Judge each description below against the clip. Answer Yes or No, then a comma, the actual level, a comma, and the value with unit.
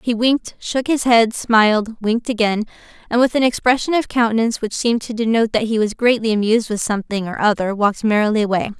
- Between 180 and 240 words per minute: Yes, fast, 205 wpm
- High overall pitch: Yes, high, 225 Hz